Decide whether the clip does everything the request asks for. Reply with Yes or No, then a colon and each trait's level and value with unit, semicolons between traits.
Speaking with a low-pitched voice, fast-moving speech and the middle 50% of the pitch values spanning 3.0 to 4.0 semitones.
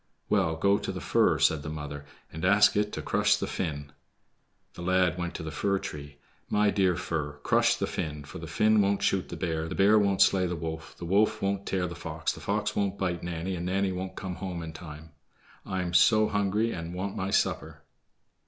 Yes: very low, 90 Hz; fast, 220 wpm; average, 3.6 semitones